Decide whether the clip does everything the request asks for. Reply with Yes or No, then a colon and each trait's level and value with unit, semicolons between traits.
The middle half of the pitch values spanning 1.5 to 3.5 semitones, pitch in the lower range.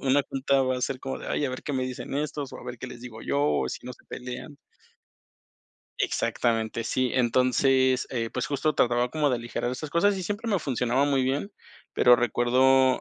Yes: narrow, 2.4 semitones; low, 130 Hz